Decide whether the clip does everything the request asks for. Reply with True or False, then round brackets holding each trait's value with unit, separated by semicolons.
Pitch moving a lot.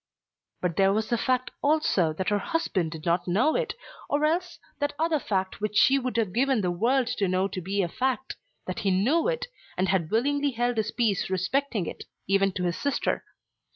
True (6.5 semitones)